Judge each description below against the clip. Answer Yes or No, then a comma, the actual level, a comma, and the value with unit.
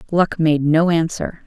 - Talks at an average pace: Yes, average, 165 wpm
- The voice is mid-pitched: Yes, medium, 160 Hz